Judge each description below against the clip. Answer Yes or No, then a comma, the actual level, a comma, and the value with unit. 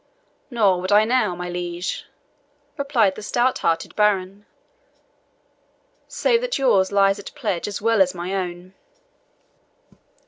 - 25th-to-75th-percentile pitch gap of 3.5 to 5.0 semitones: Yes, average, 3.8 semitones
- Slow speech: Yes, slow, 130 wpm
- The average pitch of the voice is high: Yes, high, 195 Hz